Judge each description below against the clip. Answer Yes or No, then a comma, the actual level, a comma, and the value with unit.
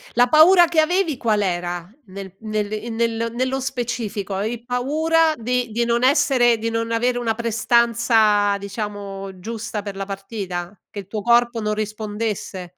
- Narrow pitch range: No, average, 3.0 semitones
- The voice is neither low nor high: No, high, 225 Hz